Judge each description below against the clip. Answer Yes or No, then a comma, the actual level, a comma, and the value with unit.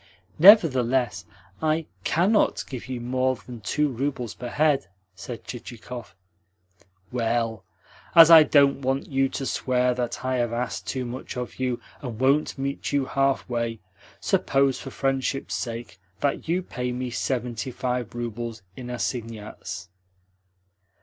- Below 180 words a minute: Yes, slow, 135 wpm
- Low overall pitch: Yes, low, 125 Hz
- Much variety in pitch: No, narrow, 2.4 semitones